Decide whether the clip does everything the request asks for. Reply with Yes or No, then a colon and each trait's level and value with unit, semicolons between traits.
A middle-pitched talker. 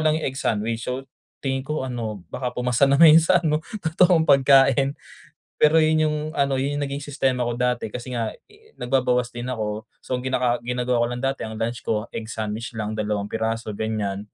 No: low, 125 Hz